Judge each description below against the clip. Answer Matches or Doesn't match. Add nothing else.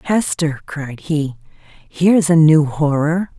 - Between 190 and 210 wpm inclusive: Doesn't match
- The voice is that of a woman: Matches